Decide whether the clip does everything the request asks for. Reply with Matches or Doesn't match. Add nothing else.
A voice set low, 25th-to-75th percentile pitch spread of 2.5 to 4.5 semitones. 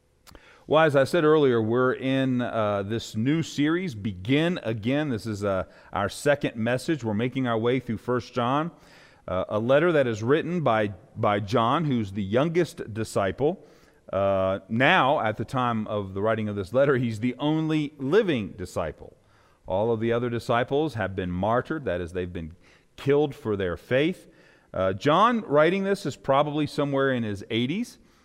Doesn't match